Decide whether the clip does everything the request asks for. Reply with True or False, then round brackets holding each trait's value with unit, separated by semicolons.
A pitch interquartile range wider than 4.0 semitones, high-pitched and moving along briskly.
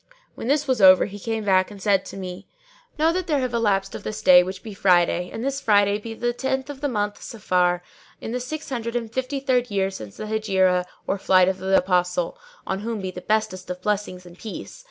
True (4.4 semitones; 205 Hz; 235 wpm)